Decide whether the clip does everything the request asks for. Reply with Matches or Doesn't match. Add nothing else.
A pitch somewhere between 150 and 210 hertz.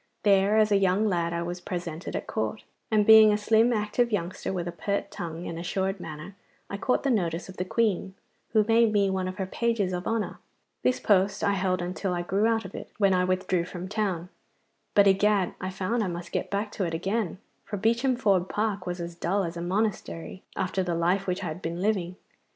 Matches